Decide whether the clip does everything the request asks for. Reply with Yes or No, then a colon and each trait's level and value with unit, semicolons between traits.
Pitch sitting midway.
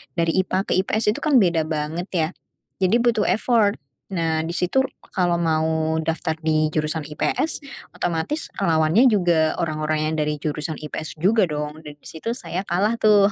Yes: medium, 165 Hz